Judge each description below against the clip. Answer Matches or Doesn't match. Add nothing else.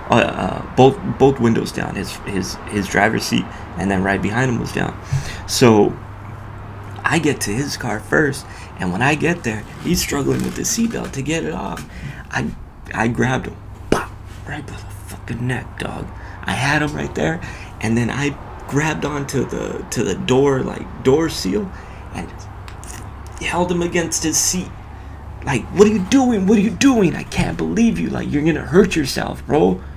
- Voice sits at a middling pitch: Doesn't match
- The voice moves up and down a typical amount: Doesn't match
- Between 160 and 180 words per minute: Doesn't match